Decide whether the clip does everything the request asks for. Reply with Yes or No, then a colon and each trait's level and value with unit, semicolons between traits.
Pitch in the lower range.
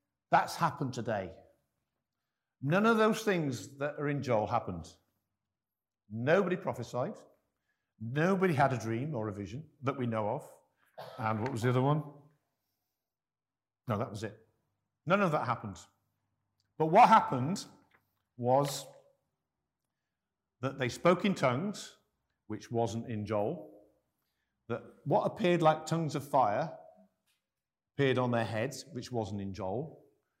Yes: low, 125 Hz